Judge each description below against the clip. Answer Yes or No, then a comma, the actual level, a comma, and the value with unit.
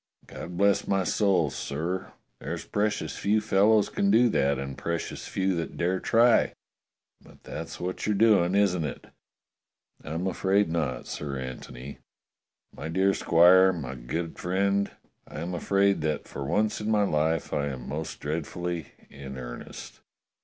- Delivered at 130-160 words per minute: Yes, average, 150 wpm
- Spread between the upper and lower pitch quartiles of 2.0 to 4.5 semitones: No, average, 5.0 semitones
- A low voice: Yes, very low, 90 Hz